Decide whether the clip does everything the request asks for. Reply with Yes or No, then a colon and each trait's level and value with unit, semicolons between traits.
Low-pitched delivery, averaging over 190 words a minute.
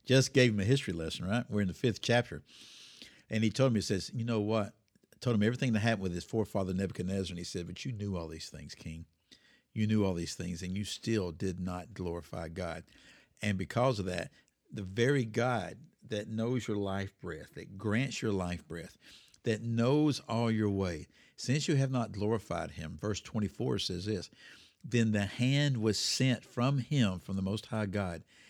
Yes: low, 105 Hz; fast, 205 wpm